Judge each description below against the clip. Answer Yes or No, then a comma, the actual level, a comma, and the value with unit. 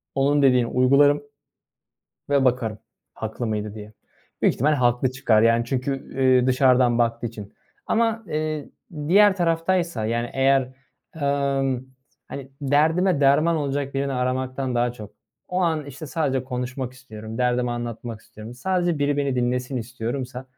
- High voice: No, low, 130 Hz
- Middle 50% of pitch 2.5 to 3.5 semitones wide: Yes, average, 2.9 semitones